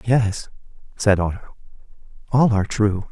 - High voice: No, low, 105 Hz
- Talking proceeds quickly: No, slow, 115 wpm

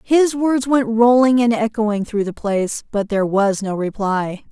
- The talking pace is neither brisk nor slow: Yes, average, 185 wpm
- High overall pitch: Yes, high, 225 Hz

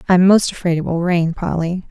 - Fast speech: Yes, fast, 220 wpm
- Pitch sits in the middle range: Yes, medium, 175 Hz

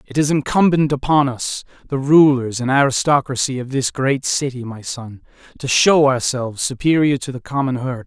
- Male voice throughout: Yes, male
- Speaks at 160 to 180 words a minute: Yes, average, 170 wpm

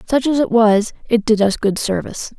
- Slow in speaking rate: No, fast, 225 wpm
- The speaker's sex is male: No, female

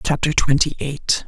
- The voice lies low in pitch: No, medium, 145 Hz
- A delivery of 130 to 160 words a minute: Yes, average, 140 wpm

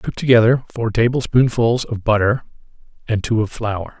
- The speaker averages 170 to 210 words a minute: No, average, 150 wpm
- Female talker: No, male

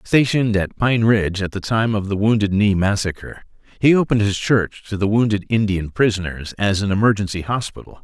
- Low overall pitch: Yes, low, 105 Hz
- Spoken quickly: No, average, 185 wpm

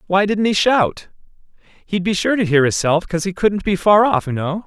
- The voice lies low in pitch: No, medium, 185 Hz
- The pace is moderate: No, fast, 245 wpm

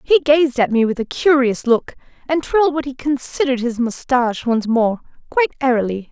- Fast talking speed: No, average, 185 wpm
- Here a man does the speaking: No, female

